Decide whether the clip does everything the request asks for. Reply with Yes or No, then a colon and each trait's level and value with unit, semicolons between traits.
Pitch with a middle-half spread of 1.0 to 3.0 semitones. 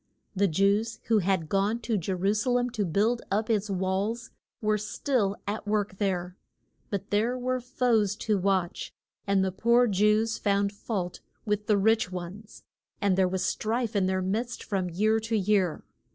Yes: average, 2.7 semitones